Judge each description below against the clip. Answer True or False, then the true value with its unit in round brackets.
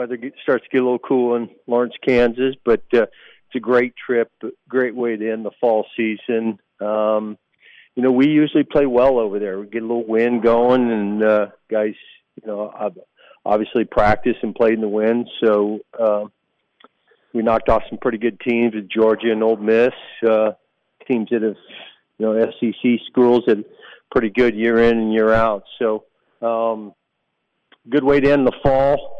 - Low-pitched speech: True (115 Hz)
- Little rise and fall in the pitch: True (2.2 semitones)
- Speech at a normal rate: True (180 wpm)